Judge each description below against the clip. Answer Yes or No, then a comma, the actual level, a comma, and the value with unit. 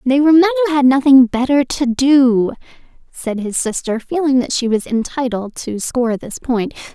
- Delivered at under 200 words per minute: Yes, average, 180 wpm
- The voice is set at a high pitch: Yes, very high, 260 Hz